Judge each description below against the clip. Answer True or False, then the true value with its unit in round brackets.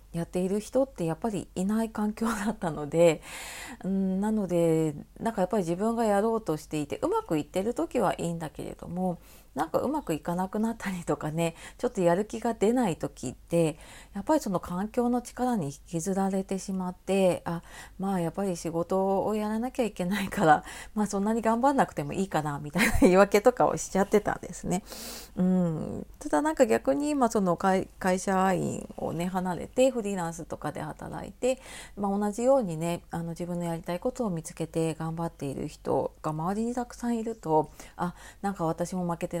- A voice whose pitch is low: False (190 Hz)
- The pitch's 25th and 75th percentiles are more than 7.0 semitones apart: False (5.1 semitones)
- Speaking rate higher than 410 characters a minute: False (395 characters per minute)